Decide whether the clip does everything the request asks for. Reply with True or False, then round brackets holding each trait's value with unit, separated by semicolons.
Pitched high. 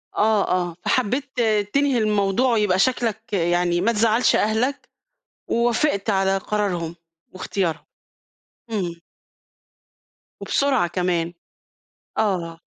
True (205 Hz)